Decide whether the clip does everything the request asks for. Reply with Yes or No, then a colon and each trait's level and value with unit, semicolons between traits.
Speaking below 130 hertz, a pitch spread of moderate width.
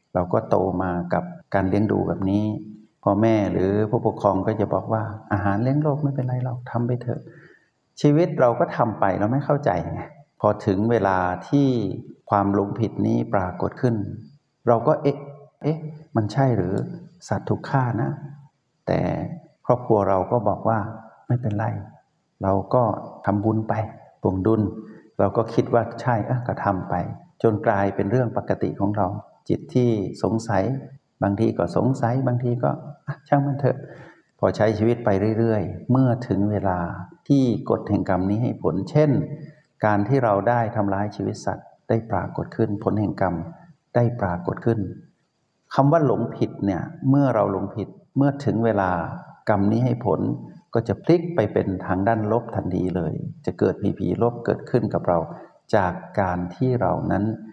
Yes: low, 110 Hz; average, 4.5 semitones